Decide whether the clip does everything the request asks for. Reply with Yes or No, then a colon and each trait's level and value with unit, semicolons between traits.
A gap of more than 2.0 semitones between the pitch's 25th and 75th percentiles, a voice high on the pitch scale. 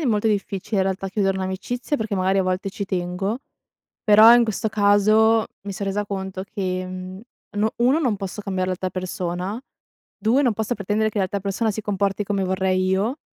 Yes: narrow, 2.4 semitones; high, 200 Hz